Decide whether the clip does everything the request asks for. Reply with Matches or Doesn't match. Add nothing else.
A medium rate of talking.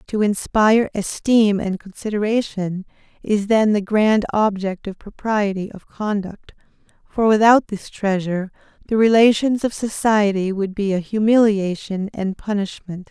Doesn't match